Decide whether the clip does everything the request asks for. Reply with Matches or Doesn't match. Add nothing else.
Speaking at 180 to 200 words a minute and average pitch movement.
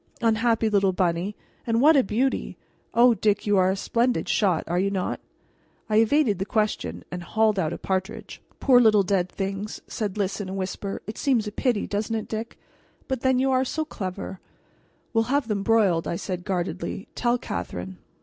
Matches